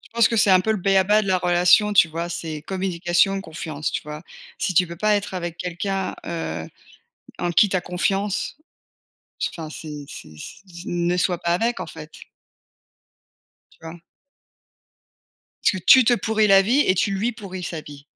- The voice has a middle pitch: Yes, medium, 180 Hz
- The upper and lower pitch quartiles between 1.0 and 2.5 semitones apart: No, average, 2.9 semitones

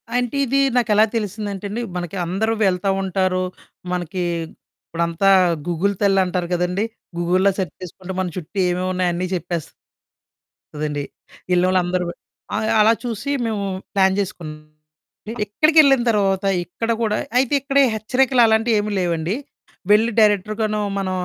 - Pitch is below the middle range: No, high, 195 Hz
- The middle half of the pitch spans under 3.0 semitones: No, average, 3.4 semitones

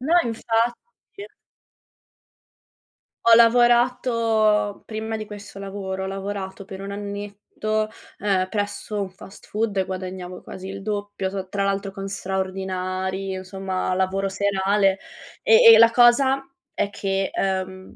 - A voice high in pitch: Yes, high, 200 Hz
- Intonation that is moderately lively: No, narrow, 2.2 semitones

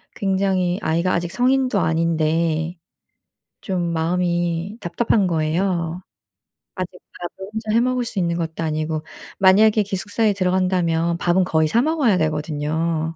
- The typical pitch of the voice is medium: Yes, medium, 175 Hz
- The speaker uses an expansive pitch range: No, average, 3.3 semitones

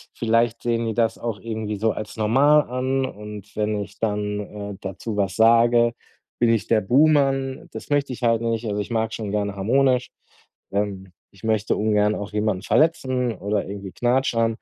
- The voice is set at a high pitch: No, low, 110 Hz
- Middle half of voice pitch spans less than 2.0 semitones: No, average, 2.7 semitones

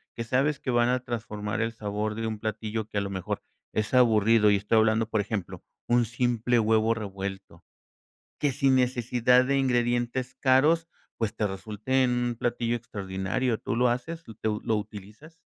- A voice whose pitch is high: No, low, 115 Hz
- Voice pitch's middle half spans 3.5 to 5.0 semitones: No, average, 2.8 semitones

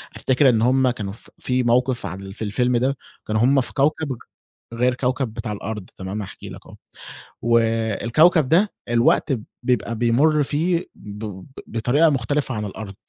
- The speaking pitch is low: Yes, low, 120 Hz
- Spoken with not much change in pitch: No, average, 3.5 semitones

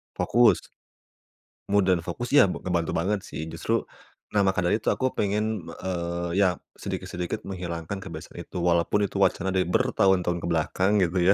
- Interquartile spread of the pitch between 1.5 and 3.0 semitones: Yes, narrow, 2.6 semitones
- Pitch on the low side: Yes, very low, 95 Hz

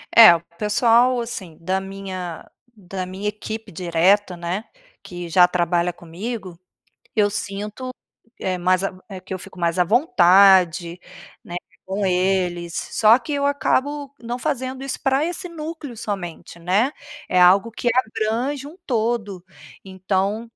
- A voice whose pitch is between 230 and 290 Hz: No, high, 195 Hz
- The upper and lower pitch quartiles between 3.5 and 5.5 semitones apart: Yes, average, 4.8 semitones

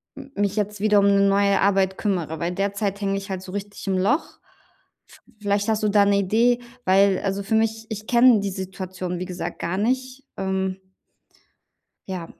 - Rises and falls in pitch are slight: Yes, narrow, 1.9 semitones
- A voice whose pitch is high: Yes, high, 200 Hz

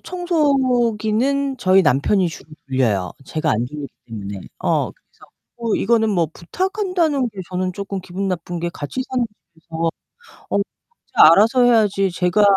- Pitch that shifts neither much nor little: No, wide, 7.1 semitones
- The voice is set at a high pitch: Yes, high, 200 Hz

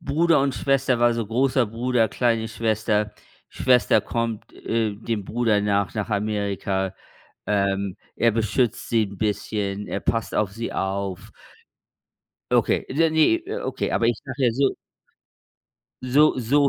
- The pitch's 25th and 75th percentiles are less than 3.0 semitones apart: No, average, 3.3 semitones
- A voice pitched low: Yes, low, 115 Hz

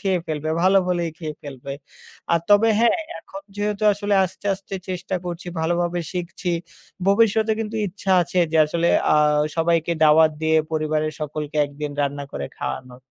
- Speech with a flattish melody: No, average, 4.1 semitones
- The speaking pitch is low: No, medium, 170 Hz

